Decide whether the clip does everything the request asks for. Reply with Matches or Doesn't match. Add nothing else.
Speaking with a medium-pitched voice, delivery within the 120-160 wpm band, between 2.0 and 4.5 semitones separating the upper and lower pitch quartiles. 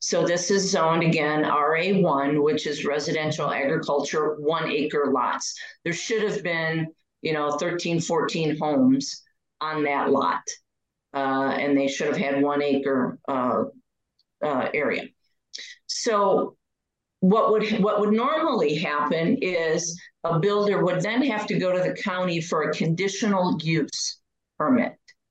Doesn't match